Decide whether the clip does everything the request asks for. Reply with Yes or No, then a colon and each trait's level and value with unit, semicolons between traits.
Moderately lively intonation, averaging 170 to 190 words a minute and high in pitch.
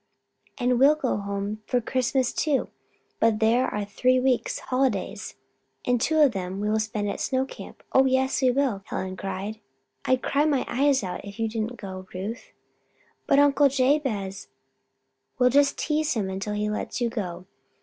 Yes: average, 4.5 semitones; average, 175 wpm; high, 240 Hz